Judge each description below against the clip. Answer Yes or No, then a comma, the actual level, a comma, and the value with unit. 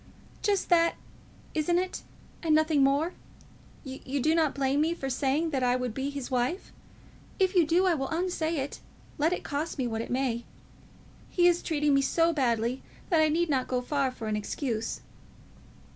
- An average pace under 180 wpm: No, average, 185 wpm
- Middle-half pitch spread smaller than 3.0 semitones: No, average, 4.3 semitones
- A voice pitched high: Yes, very high, 290 Hz